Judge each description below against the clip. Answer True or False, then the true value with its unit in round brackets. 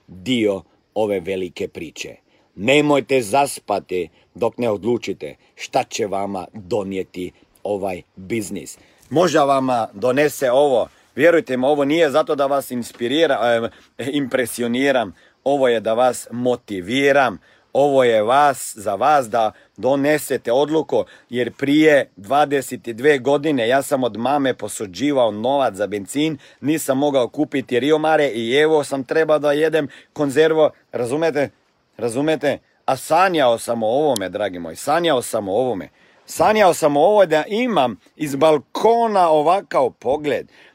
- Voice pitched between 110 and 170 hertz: True (140 Hz)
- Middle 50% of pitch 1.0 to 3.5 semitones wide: False (4.1 semitones)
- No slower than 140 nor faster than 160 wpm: False (130 wpm)